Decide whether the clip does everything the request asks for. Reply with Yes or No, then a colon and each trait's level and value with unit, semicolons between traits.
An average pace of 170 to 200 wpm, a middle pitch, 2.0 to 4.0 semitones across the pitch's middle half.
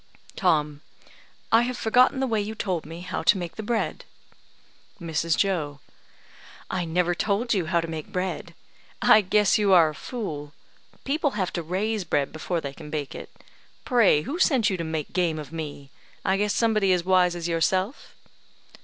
No: average, 180 wpm; medium, 180 Hz; average, 4.7 semitones